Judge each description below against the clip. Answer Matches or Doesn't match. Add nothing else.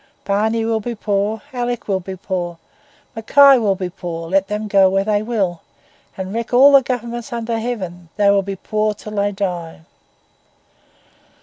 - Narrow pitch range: Doesn't match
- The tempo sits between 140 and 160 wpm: Doesn't match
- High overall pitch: Matches